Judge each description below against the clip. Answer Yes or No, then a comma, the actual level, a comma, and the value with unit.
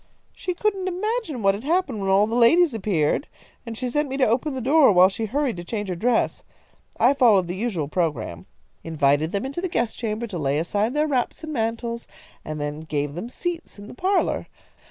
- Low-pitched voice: No, high, 225 Hz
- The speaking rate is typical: No, fast, 210 wpm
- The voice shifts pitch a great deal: Yes, wide, 8.0 semitones